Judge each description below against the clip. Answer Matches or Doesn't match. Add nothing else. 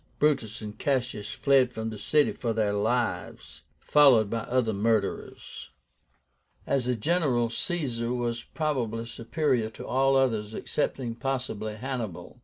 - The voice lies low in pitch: Matches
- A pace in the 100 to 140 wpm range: Matches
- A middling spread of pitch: Matches